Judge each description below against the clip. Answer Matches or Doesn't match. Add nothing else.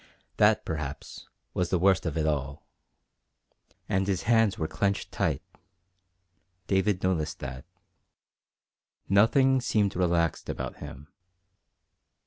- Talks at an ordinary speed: Doesn't match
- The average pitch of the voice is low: Matches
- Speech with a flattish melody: Doesn't match